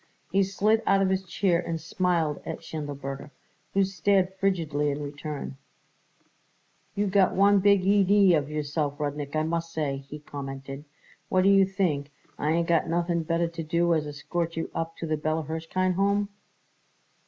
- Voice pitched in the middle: Yes, medium, 165 Hz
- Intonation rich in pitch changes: No, average, 4.2 semitones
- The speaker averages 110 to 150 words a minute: No, average, 165 wpm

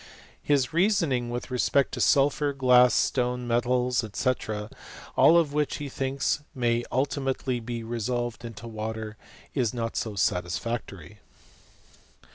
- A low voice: Yes, low, 125 Hz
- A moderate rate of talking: No, slow, 130 wpm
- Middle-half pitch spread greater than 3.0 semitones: No, average, 2.7 semitones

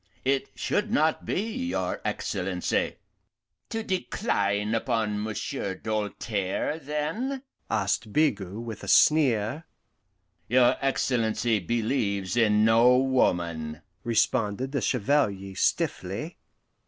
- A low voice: Yes, low, 115 Hz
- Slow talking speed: Yes, slow, 95 wpm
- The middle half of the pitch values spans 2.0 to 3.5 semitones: No, average, 5.3 semitones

